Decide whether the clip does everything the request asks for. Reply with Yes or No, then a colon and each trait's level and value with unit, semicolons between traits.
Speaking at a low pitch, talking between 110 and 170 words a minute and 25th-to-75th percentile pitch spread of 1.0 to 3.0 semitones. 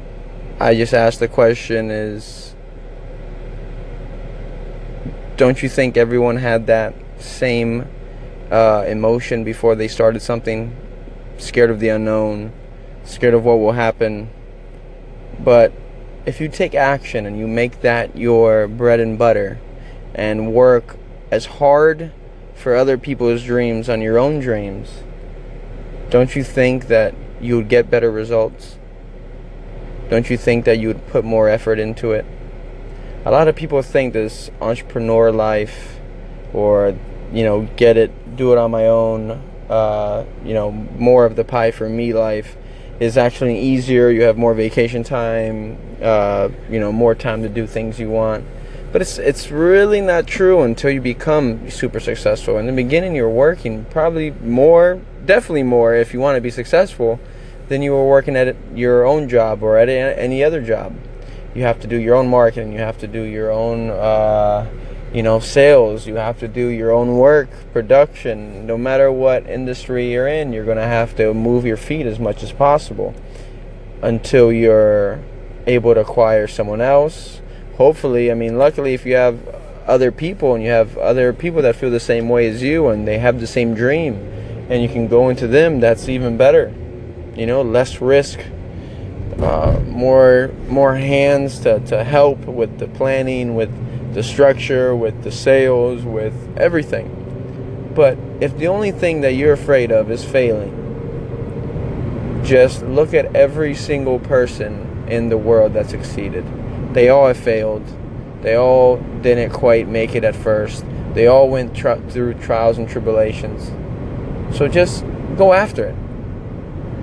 Yes: low, 120 Hz; average, 160 wpm; narrow, 2.5 semitones